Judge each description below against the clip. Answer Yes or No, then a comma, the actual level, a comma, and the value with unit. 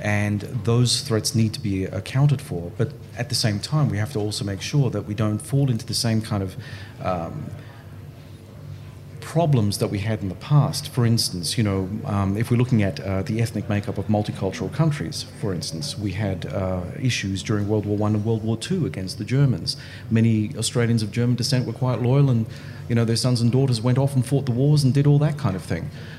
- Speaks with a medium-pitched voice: No, low, 115 Hz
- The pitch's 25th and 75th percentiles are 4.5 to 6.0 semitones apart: No, average, 3.7 semitones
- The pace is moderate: No, fast, 220 wpm